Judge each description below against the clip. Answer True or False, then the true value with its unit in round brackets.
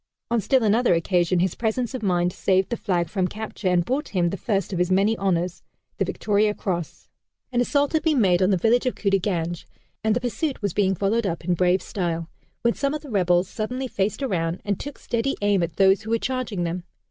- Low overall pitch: False (200 Hz)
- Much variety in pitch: False (4.7 semitones)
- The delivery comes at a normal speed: False (220 wpm)